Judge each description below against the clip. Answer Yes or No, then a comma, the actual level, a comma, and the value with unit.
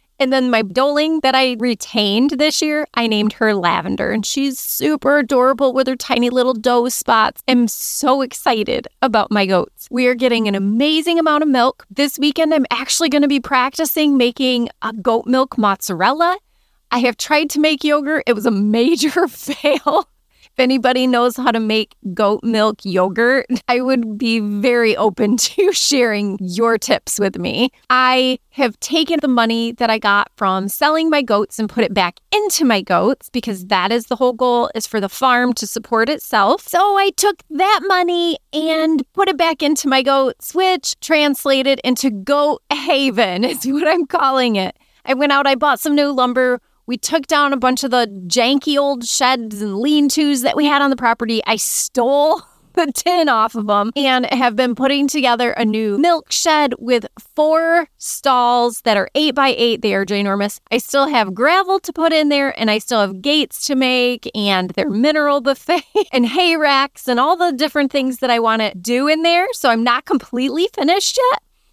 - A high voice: Yes, very high, 255 Hz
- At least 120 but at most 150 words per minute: No, average, 190 wpm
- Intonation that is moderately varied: Yes, average, 4.3 semitones